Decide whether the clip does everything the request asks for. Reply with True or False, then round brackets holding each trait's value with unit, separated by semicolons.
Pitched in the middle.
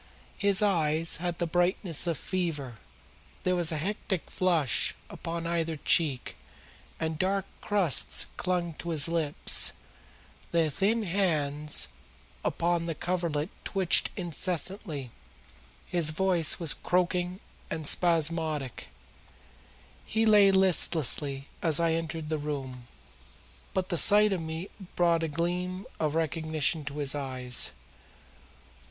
True (165 Hz)